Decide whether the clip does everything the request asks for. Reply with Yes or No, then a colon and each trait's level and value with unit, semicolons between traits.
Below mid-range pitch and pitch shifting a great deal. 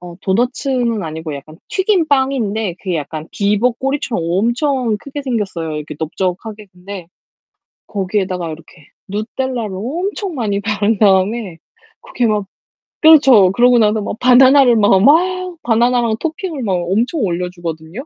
No: high, 215 Hz; wide, 5.8 semitones